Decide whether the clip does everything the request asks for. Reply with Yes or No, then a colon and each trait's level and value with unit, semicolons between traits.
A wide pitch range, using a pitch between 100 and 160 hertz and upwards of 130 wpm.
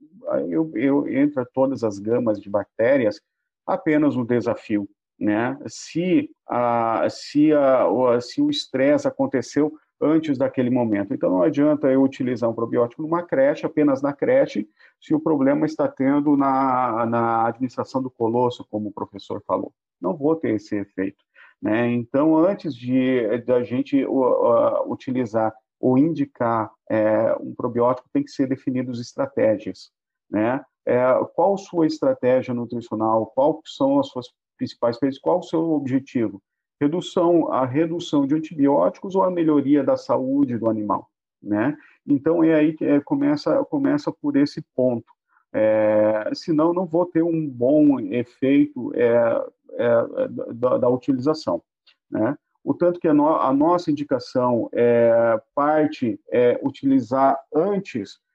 Yes: wide, 5.9 semitones; medium, 140 Hz; average, 145 wpm